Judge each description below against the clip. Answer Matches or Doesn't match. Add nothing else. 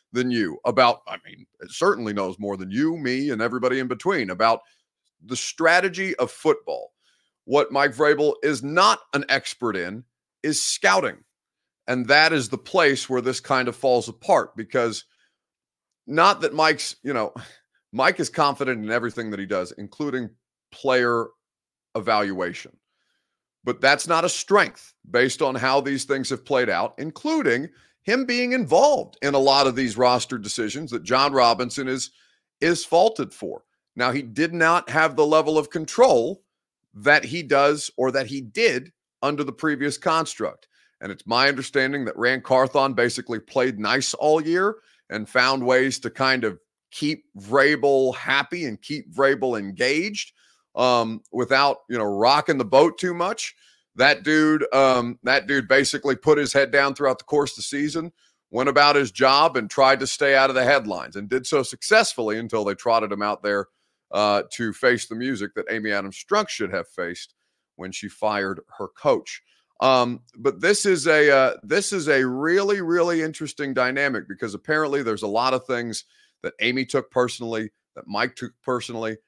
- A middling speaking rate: Matches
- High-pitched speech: Doesn't match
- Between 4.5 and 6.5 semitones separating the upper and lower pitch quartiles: Doesn't match